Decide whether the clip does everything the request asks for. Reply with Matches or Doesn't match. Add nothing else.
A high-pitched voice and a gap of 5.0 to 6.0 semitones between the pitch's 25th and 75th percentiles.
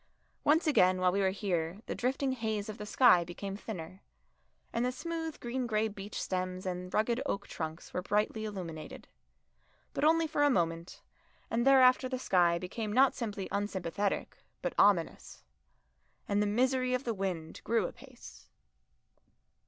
Matches